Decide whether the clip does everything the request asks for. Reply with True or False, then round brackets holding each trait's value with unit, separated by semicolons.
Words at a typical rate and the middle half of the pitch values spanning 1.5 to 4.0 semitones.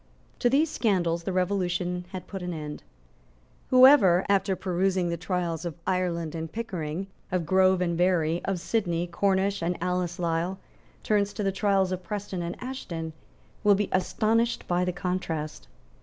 True (155 wpm; 2.4 semitones)